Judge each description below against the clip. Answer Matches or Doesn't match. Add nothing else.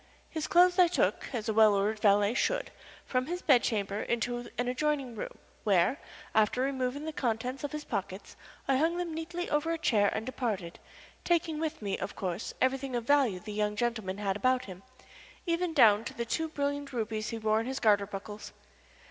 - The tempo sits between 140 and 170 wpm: Doesn't match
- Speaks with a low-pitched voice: Doesn't match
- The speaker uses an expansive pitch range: Matches